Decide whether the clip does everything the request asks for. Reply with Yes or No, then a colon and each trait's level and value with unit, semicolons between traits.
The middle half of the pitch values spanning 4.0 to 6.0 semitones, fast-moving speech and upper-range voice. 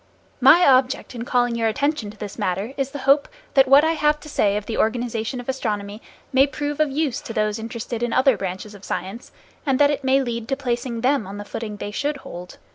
Yes: average, 4.4 semitones; fast, 230 wpm; high, 245 Hz